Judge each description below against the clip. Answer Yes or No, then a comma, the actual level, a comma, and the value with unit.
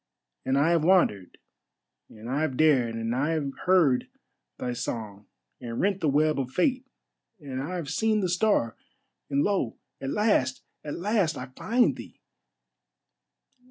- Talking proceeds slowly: No, average, 155 wpm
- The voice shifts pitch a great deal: Yes, wide, 6.3 semitones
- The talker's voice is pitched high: No, medium, 145 Hz